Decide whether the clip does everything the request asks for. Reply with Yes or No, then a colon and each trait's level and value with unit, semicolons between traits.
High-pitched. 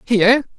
Yes: high, 230 Hz